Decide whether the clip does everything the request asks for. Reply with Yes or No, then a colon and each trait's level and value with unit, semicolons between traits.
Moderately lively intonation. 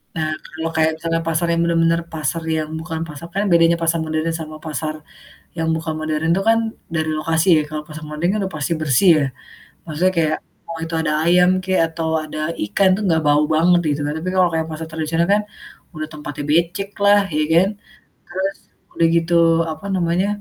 No: narrow, 1.7 semitones